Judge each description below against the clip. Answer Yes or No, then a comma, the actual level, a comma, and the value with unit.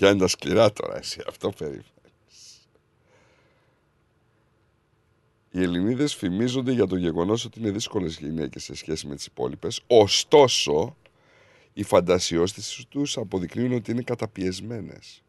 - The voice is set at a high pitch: No, low, 105 Hz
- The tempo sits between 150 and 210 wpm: No, average, 120 wpm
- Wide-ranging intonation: No, average, 4.6 semitones